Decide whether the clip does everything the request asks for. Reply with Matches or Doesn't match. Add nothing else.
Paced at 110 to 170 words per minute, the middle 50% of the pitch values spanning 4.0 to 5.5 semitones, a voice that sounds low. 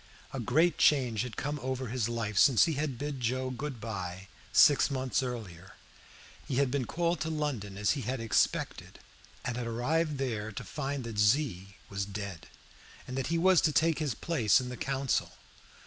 Doesn't match